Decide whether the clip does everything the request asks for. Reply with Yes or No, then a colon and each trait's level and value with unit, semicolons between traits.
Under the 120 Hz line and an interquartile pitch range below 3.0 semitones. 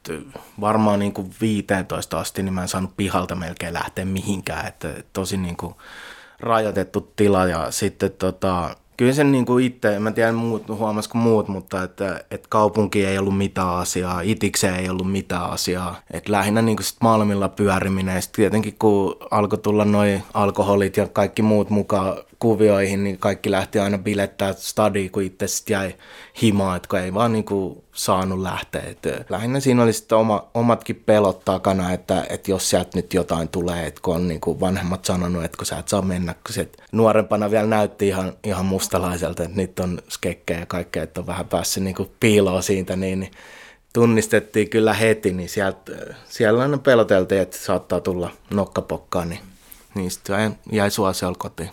Yes: low, 100 Hz; narrow, 2.4 semitones